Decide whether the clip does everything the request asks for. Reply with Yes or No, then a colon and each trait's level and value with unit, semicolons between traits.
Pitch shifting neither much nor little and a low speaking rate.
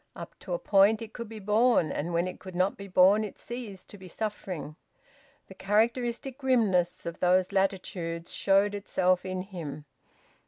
No: average, 3.1 semitones; average, 170 wpm